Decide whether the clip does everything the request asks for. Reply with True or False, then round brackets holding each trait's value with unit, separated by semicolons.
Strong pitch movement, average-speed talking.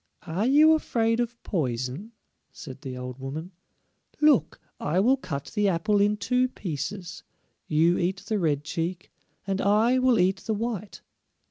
True (6.4 semitones; 150 wpm)